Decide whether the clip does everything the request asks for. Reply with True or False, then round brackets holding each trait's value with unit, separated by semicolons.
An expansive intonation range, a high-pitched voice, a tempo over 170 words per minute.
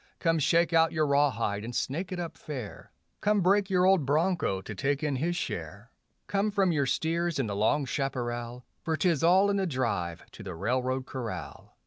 False (6.3 semitones; 145 Hz; 190 wpm)